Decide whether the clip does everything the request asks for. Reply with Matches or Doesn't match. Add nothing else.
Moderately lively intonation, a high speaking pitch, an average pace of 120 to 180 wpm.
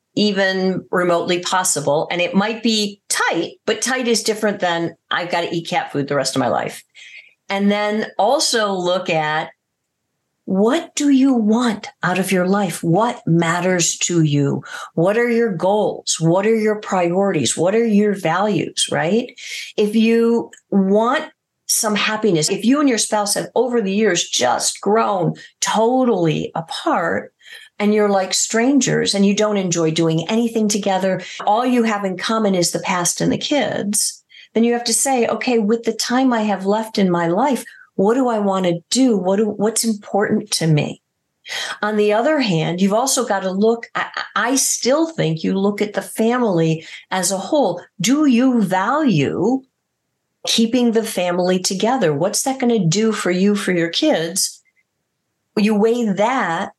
Matches